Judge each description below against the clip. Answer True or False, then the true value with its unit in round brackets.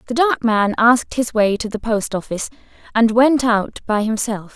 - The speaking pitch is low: False (225 Hz)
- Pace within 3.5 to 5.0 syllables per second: True (4.9 syllables/s)